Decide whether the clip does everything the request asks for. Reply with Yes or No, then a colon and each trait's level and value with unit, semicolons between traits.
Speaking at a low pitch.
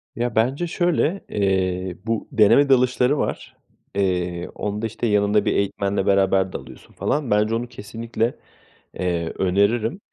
Yes: low, 105 Hz